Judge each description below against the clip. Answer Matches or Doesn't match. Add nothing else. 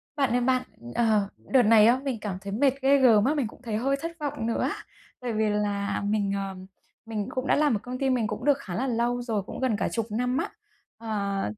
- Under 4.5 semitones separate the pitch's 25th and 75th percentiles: Matches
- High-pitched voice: Matches